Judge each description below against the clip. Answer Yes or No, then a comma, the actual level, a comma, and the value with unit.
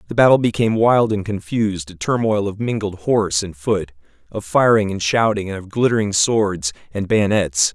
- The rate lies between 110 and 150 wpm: No, average, 180 wpm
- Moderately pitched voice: No, low, 100 Hz